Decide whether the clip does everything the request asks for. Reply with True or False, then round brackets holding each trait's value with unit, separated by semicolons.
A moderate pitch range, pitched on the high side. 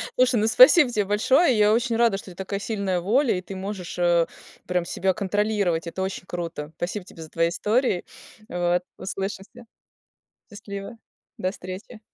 True (3.6 semitones; 195 Hz)